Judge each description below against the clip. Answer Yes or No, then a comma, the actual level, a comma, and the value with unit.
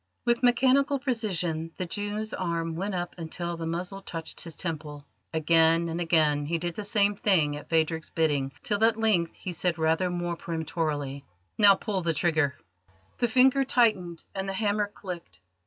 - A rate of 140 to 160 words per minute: No, average, 170 wpm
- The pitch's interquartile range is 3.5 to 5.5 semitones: Yes, average, 4.1 semitones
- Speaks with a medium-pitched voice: Yes, medium, 175 Hz